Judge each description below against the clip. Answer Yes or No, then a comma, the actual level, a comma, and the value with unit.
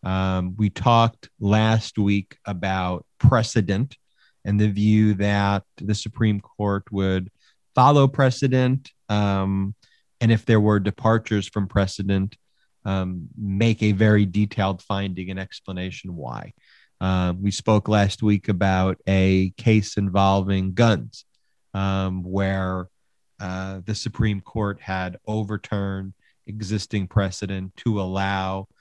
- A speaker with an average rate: No, slow, 115 wpm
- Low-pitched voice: Yes, low, 100 Hz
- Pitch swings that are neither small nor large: No, narrow, 2.1 semitones